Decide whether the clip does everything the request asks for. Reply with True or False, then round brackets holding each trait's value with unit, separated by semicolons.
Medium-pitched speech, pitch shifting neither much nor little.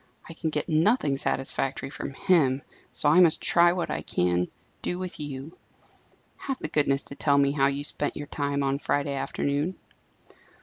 True (145 Hz; 3.0 semitones)